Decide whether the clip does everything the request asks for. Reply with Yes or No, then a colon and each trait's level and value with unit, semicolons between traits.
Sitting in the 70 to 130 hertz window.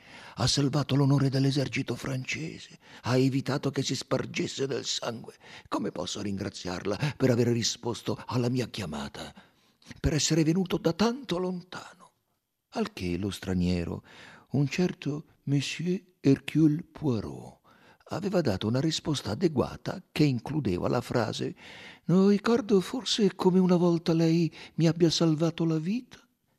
No: medium, 140 Hz